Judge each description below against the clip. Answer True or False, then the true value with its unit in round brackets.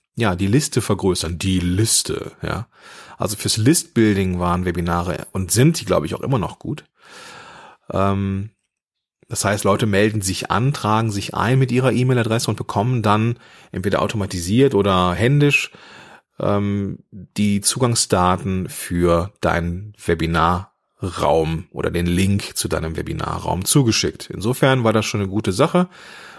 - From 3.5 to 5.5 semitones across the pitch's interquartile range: True (4.4 semitones)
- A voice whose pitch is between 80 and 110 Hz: True (100 Hz)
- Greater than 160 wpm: False (135 wpm)